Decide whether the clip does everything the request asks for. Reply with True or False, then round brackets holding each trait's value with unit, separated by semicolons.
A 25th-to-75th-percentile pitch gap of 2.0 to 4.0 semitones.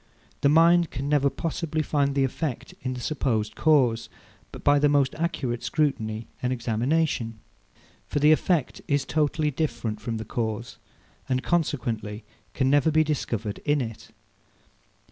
False (4.6 semitones)